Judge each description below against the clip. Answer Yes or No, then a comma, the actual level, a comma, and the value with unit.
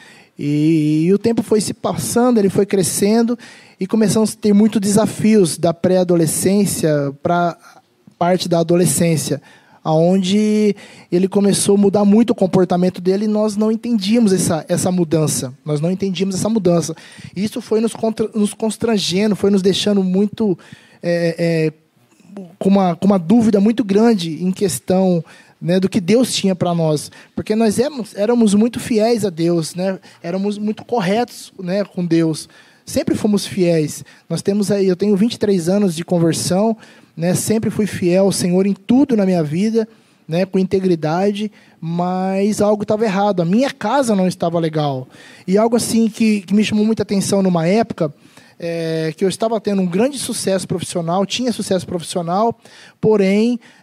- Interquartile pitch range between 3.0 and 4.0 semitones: Yes, average, 3.6 semitones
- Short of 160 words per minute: No, average, 165 wpm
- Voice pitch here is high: Yes, high, 195 Hz